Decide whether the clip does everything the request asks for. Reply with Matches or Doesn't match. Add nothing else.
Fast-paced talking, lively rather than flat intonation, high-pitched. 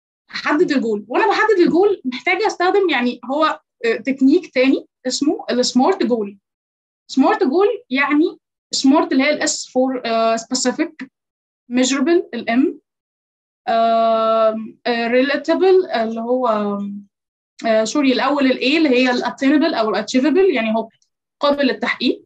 Doesn't match